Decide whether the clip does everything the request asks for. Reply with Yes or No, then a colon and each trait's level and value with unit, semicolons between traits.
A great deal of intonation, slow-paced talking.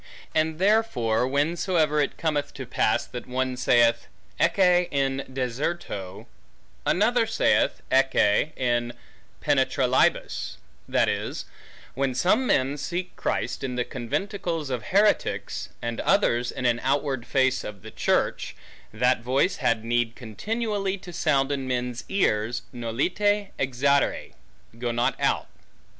Yes: wide, 6.1 semitones; slow, 125 wpm